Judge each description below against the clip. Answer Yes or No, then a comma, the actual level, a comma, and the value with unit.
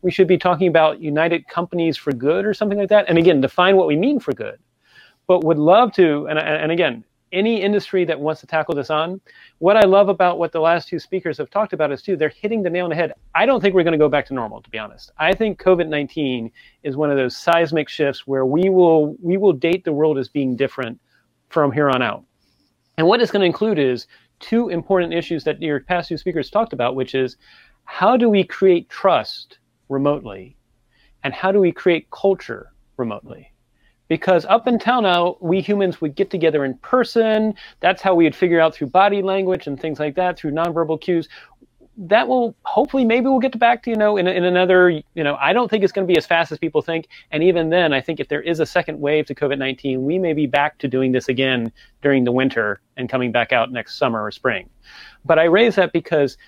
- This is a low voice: No, medium, 170 Hz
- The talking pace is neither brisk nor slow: No, fast, 235 wpm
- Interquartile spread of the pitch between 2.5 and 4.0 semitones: No, average, 4.4 semitones